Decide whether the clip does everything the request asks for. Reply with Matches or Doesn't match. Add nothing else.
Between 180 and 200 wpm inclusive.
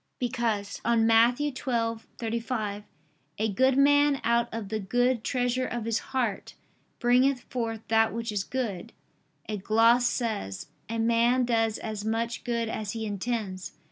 Doesn't match